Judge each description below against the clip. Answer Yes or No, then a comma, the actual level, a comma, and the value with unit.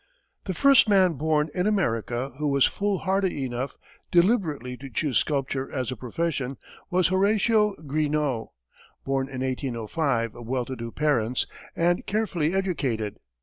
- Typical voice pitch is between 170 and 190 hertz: No, medium, 145 Hz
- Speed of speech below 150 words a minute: Yes, average, 140 wpm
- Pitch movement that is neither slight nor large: No, wide, 6.4 semitones